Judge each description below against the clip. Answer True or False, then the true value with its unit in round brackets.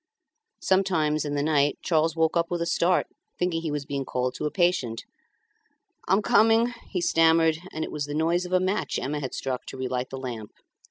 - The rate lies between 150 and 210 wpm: True (205 wpm)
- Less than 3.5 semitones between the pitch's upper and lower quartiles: False (3.8 semitones)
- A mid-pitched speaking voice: True (160 Hz)